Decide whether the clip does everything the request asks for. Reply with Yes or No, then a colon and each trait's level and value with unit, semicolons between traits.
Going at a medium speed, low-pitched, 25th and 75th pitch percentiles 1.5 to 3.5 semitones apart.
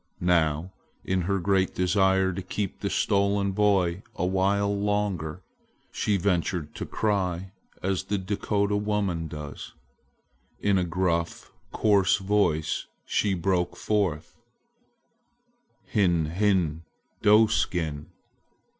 No: slow, 105 wpm; very low, 95 Hz; average, 2.7 semitones